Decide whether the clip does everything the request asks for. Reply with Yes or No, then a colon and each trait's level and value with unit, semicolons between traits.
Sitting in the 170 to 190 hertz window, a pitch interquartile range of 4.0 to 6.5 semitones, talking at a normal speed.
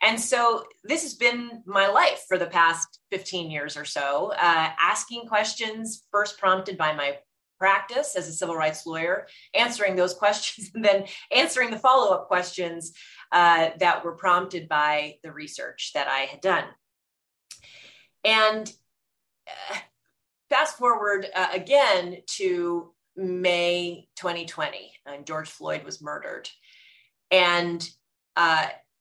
No: medium, 185 Hz; average, 4.5 semitones; slow, 130 wpm